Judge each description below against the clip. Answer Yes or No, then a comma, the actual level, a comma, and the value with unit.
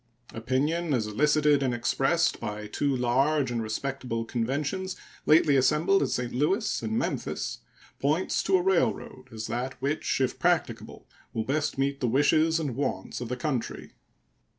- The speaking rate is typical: Yes, average, 150 wpm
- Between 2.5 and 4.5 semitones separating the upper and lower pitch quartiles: Yes, average, 4.0 semitones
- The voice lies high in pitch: No, low, 135 Hz